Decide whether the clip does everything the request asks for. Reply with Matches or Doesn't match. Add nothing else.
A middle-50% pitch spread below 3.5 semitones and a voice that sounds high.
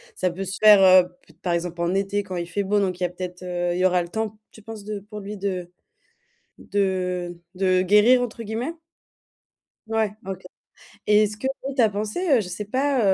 Matches